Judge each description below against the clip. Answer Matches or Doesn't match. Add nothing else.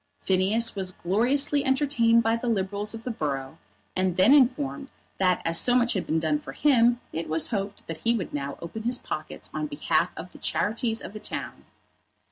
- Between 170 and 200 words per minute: Matches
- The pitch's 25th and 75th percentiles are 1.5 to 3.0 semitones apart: Doesn't match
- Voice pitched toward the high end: Matches